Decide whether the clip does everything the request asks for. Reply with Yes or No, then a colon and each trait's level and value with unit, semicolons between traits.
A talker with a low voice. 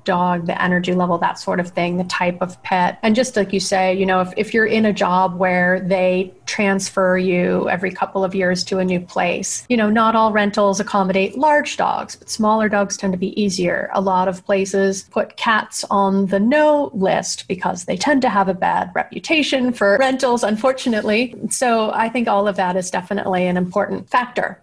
No: high, 195 Hz